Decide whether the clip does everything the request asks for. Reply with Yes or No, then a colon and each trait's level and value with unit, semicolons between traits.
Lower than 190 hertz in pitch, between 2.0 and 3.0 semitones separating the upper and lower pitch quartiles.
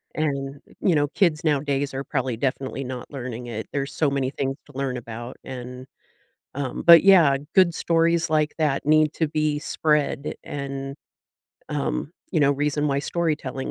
Yes: medium, 140 Hz; narrow, 2.4 semitones